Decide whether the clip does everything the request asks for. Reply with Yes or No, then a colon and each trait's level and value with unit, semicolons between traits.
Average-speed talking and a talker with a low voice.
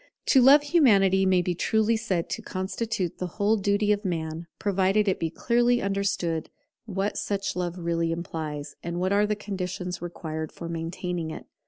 No: average, 170 wpm; medium, 185 Hz